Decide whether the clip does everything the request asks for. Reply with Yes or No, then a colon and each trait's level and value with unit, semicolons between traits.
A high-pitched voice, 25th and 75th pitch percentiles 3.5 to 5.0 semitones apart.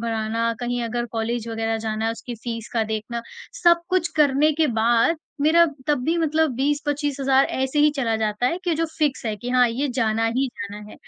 Yes: high, 245 Hz; average, 4.5 semitones